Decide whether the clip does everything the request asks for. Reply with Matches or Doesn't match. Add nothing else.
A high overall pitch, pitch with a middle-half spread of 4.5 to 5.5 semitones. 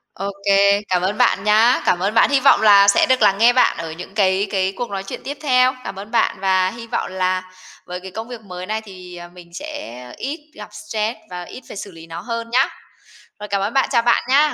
Doesn't match